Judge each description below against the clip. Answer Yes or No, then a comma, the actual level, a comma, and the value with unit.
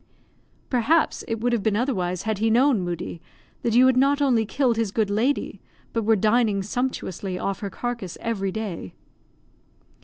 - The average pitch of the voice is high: Yes, high, 225 Hz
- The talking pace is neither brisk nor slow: Yes, average, 165 wpm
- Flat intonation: No, average, 3.7 semitones